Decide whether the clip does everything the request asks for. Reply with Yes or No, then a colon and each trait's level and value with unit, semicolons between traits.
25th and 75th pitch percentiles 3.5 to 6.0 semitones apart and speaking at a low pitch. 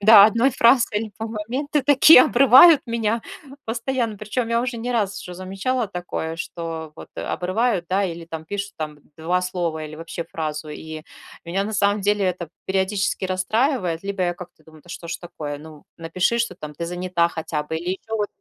No: average, 5.3 semitones; high, 190 Hz